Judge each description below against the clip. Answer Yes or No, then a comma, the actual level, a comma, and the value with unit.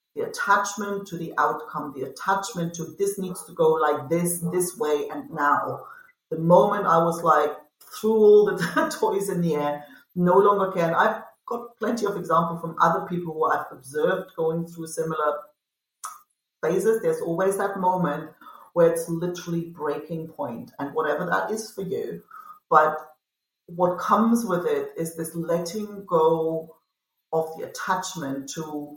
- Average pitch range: Yes, average, 4.1 semitones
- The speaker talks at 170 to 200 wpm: No, average, 160 wpm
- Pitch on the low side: No, medium, 170 Hz